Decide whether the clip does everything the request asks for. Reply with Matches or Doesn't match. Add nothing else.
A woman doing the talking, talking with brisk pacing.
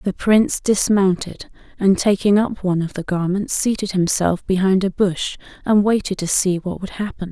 Doesn't match